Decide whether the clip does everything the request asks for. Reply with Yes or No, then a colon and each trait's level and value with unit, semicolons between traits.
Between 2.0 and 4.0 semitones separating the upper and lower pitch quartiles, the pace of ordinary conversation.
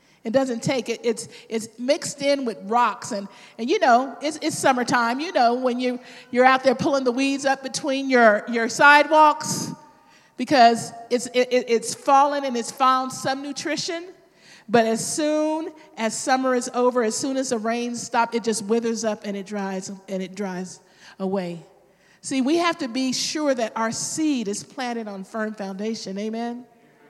Yes: average, 3.6 semitones; average, 180 wpm